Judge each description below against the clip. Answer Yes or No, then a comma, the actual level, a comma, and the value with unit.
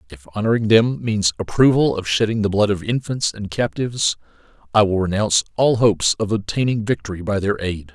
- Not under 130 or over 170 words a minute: No, average, 180 wpm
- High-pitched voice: No, low, 105 Hz